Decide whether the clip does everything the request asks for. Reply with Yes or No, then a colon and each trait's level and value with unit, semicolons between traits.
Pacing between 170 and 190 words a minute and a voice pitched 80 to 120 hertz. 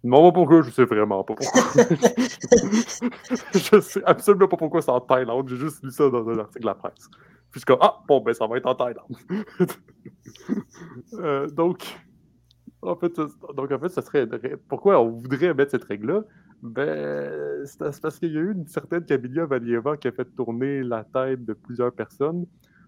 No: average, 185 wpm; medium, 140 Hz